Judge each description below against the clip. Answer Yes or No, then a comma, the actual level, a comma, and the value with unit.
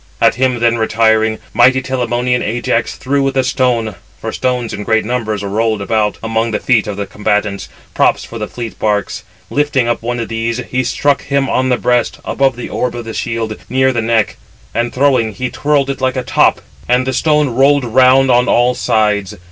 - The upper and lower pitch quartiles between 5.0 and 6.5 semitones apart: No, narrow, 2.6 semitones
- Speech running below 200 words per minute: No, fast, 205 wpm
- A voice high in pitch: No, low, 120 Hz